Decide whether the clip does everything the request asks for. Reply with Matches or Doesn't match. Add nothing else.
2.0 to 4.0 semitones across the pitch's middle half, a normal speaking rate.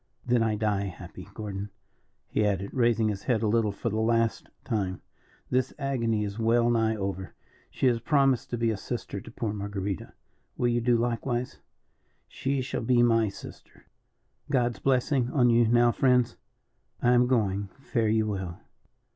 Matches